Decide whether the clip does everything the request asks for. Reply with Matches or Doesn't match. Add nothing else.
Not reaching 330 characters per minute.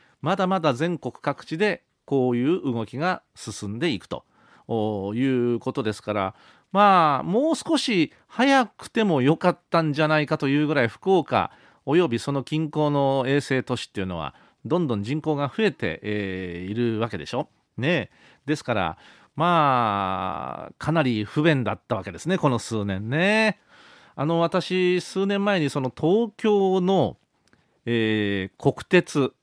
Matches